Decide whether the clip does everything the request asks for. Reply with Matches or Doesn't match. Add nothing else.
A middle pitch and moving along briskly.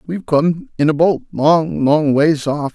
Doesn't match